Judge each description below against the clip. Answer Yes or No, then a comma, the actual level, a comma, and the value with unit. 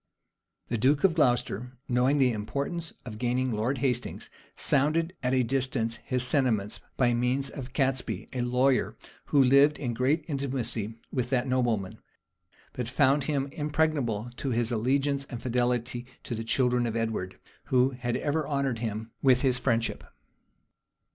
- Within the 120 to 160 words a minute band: Yes, average, 150 wpm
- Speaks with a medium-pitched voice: No, low, 125 Hz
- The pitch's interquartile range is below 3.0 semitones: Yes, narrow, 2.6 semitones